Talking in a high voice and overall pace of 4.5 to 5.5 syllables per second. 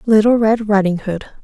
Yes: high, 210 Hz; 5.2 syllables/s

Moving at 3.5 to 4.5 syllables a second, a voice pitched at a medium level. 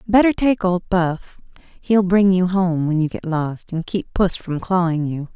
Yes: 4.1 syllables/s; medium, 180 Hz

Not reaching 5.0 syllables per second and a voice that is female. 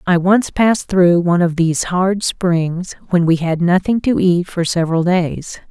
Yes: 4.5 syllables/s; female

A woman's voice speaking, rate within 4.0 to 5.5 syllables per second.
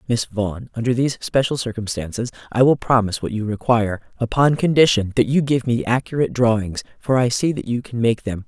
No: female; 6.0 syllables/s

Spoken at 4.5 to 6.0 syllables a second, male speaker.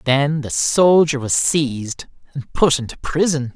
No: 4.1 syllables/s; male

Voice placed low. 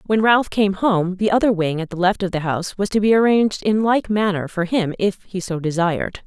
No: high, 195 Hz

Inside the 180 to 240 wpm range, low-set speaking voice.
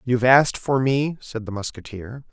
Yes: fast, 205 wpm; low, 120 Hz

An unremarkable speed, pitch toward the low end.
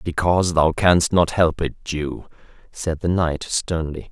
Yes: average, 160 wpm; very low, 80 Hz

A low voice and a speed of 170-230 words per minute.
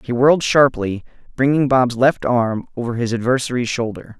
No: low, 125 Hz; average, 160 wpm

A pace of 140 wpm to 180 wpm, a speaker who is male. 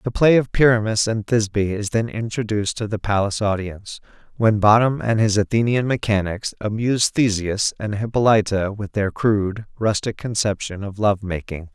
Yes: average, 160 wpm; male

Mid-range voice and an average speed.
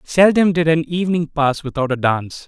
Yes: medium, 155 Hz; average, 195 wpm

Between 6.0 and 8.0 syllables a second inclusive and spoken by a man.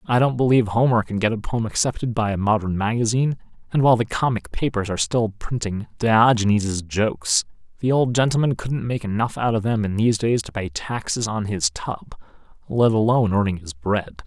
No: 5.6 syllables/s; male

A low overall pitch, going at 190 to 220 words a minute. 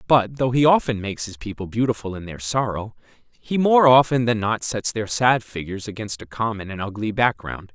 Yes: low, 110 Hz; average, 200 wpm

